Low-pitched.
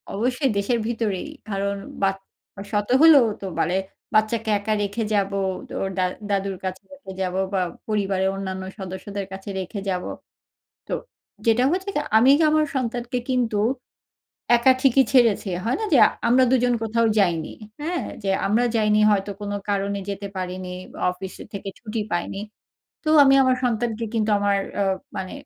No: high, 210 Hz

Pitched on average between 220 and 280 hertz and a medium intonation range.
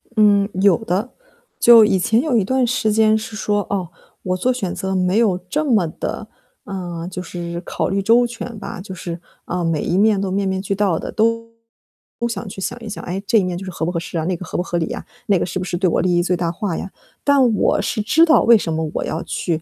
No: high, 195 Hz; average, 3.7 semitones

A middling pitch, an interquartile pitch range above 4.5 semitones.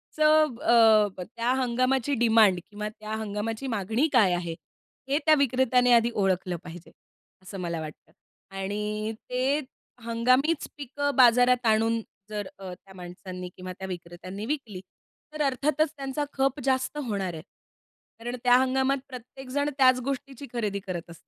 No: high, 230 Hz; average, 5.1 semitones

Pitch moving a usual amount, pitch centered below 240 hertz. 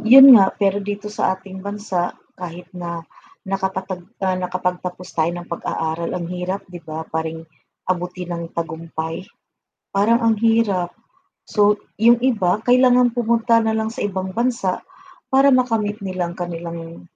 Yes: average, 4.0 semitones; high, 190 Hz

